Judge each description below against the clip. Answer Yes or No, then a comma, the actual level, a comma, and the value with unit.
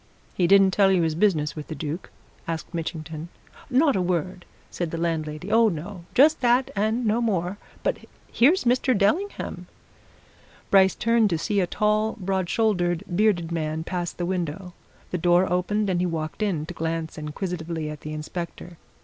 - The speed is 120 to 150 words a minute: No, average, 170 wpm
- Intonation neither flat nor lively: Yes, average, 4.3 semitones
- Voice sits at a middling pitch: Yes, medium, 180 Hz